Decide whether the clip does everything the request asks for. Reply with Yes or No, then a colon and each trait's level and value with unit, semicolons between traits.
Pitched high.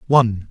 No: low, 115 Hz